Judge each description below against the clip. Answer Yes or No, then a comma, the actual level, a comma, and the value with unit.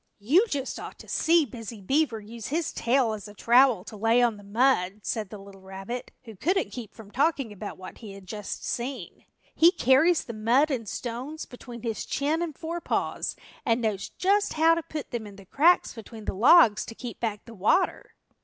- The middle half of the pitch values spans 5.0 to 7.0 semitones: Yes, average, 5.3 semitones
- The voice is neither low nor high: No, high, 235 Hz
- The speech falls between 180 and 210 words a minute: Yes, average, 200 wpm